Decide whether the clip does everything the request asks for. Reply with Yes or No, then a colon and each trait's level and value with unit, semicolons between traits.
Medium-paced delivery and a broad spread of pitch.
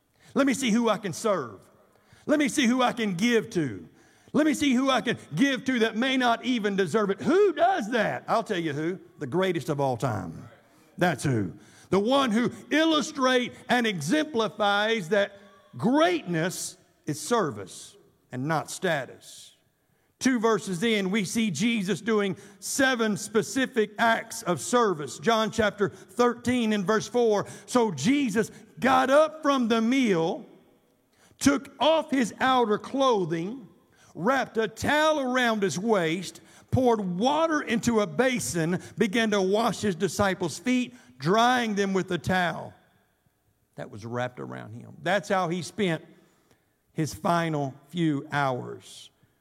Yes: average, 145 wpm; wide, 5.8 semitones